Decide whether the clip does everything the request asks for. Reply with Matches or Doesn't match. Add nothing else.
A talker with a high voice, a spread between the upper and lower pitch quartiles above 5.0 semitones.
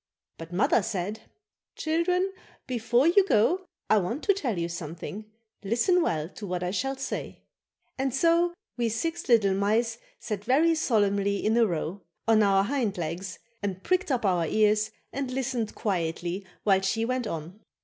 Matches